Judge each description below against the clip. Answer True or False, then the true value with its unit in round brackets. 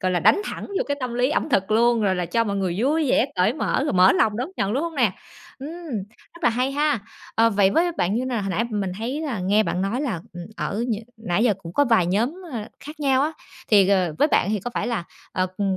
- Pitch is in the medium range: False (225 Hz)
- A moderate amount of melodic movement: False (5.7 semitones)